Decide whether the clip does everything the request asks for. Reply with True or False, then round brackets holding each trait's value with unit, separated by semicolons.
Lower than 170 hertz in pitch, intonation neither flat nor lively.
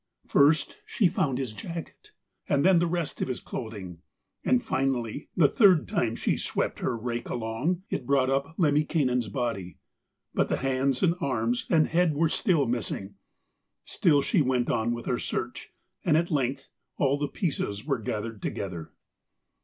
True (135 Hz; 5.0 semitones)